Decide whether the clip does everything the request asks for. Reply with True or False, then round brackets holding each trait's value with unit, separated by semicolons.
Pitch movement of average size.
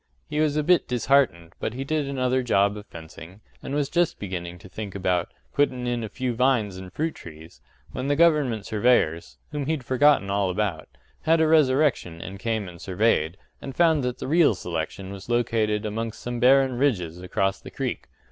False (6.5 semitones)